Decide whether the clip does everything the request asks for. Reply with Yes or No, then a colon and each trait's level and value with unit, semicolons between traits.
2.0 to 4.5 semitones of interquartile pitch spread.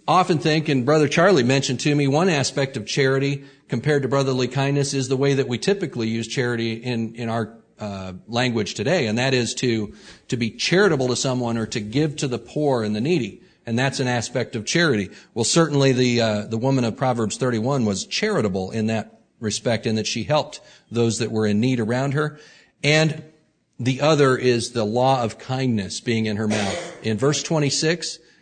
Yes: average, 3.9 semitones